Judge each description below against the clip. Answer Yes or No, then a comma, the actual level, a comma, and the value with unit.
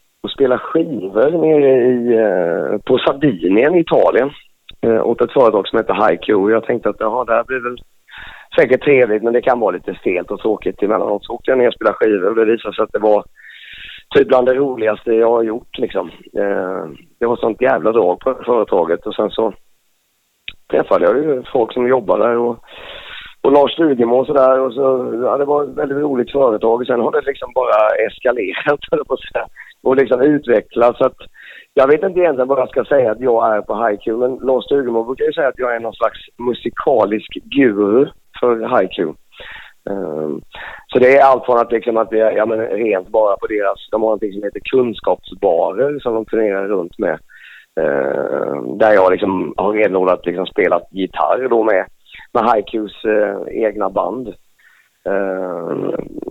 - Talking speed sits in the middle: Yes, average, 185 wpm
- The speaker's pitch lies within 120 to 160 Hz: Yes, low, 125 Hz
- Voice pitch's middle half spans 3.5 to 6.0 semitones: Yes, average, 4.0 semitones